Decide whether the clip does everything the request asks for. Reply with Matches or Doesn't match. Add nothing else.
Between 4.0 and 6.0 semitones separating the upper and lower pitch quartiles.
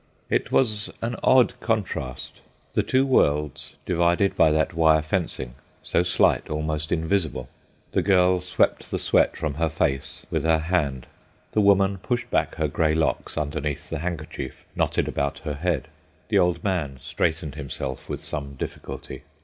Doesn't match